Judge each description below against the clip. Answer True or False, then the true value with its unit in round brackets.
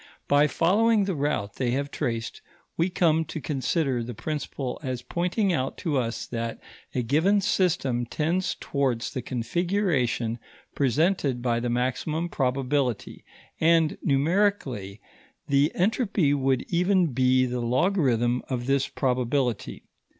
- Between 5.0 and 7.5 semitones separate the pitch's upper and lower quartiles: True (5.4 semitones)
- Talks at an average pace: False (130 wpm)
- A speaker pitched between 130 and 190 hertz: True (140 Hz)